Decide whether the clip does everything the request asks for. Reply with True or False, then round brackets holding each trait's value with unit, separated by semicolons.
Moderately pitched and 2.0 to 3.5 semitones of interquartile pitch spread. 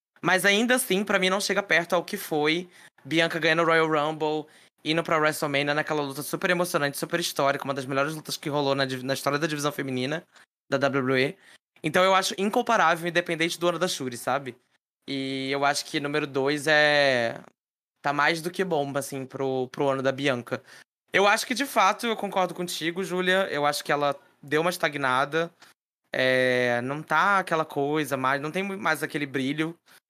False (155 Hz; 4.0 semitones)